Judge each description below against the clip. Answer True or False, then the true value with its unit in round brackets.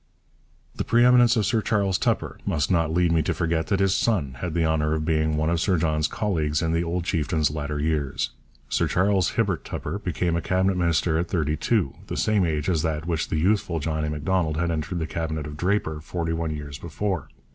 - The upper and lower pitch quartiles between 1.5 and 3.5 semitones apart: True (3.1 semitones)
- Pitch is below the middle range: True (80 Hz)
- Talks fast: True (220 wpm)